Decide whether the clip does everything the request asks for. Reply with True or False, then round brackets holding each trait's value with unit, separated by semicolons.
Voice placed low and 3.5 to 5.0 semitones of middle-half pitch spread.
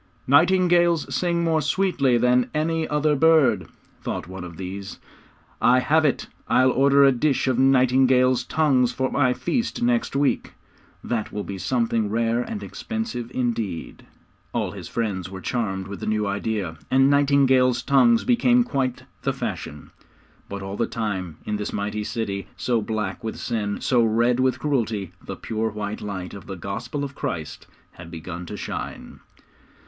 False (120 Hz; 5.6 semitones)